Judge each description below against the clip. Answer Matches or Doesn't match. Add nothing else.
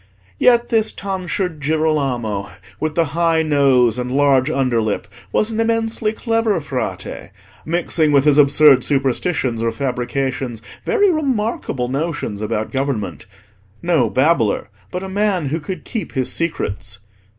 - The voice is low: Doesn't match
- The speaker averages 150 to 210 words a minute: Doesn't match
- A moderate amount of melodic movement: Doesn't match